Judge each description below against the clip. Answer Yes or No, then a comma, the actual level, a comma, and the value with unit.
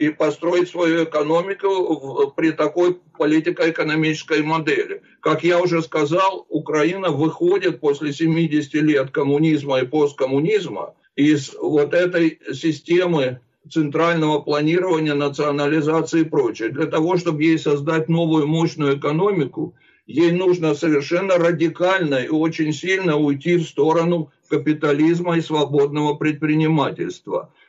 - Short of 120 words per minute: Yes, slow, 110 wpm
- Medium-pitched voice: Yes, medium, 160 Hz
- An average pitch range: No, narrow, 2.1 semitones